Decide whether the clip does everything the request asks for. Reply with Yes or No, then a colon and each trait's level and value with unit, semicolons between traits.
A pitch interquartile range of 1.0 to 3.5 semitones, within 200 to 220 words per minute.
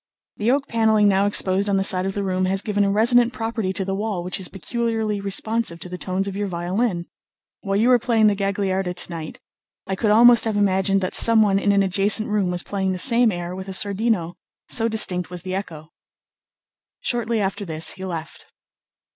Yes: average, 2.8 semitones; fast, 205 wpm